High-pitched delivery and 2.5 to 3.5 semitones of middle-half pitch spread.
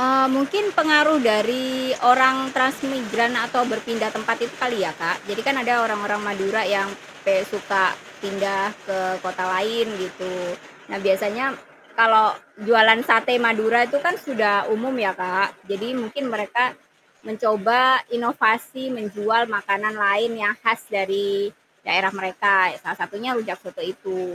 Yes: high, 220 Hz; average, 3.2 semitones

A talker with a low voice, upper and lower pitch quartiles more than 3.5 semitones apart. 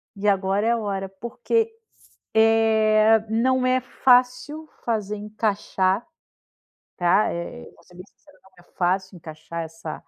No: high, 215 Hz; average, 3.9 semitones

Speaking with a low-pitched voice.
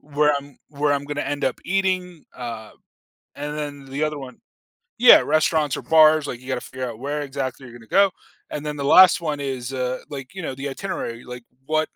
No: medium, 145 Hz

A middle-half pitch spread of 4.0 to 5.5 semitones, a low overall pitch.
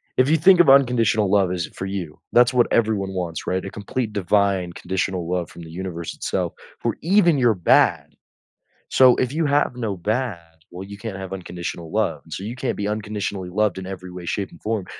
Yes: average, 4.8 semitones; low, 100 Hz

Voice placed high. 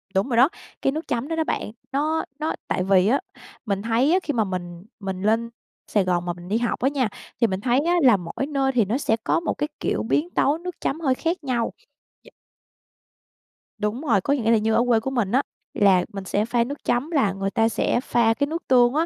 Yes: high, 235 Hz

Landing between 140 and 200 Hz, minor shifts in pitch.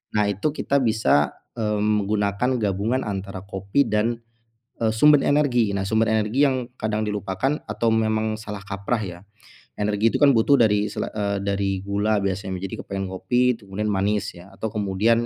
No: low, 105 Hz; narrow, 2.2 semitones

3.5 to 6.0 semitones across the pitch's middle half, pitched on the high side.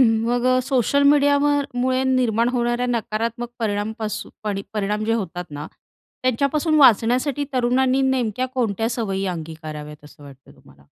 Yes: average, 4.1 semitones; high, 230 Hz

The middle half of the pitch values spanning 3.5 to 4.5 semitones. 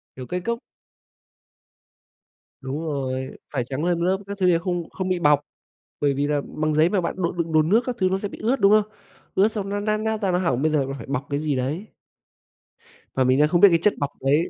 No: average, 5.3 semitones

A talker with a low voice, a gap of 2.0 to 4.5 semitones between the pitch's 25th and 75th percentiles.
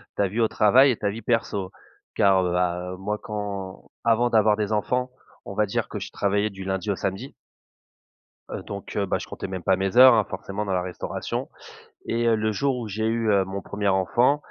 Yes: low, 105 Hz; average, 2.8 semitones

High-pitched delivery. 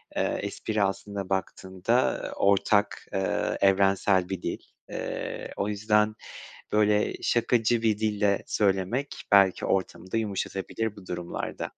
No: low, 100 Hz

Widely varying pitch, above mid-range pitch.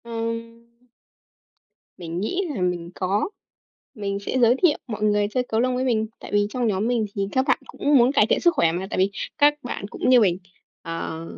No: average, 4.2 semitones; high, 220 Hz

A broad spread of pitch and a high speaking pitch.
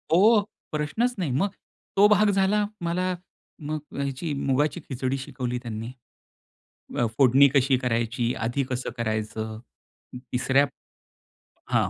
No: wide, 6.0 semitones; low, 135 Hz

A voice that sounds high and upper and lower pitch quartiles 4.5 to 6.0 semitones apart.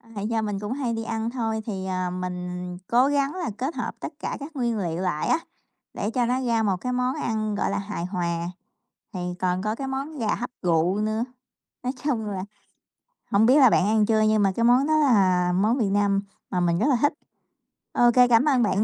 Yes: high, 215 Hz; average, 4.8 semitones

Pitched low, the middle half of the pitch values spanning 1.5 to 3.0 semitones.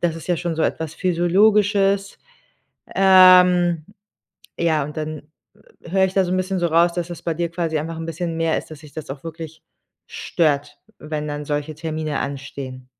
No: medium, 165 Hz; average, 2.7 semitones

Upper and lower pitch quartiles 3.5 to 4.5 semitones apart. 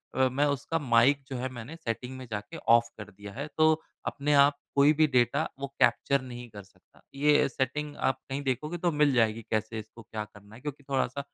Yes: average, 3.9 semitones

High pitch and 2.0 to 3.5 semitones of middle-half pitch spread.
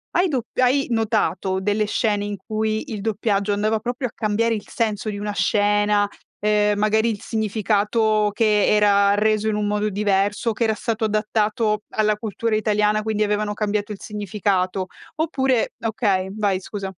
No: high, 210 Hz; narrow, 1.2 semitones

